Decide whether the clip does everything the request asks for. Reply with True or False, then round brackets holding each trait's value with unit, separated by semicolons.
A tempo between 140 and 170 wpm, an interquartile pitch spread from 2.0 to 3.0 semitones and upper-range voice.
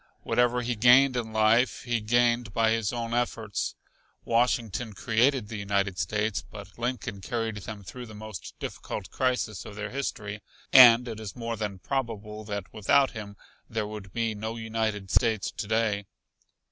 False (160 wpm; 2.4 semitones; 110 Hz)